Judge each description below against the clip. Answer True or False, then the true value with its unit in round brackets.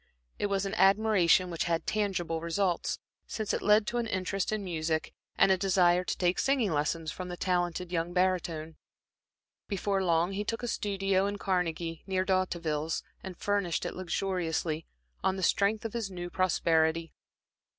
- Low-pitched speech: False (185 Hz)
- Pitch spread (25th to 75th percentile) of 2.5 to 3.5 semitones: True (2.9 semitones)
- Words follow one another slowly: False (165 wpm)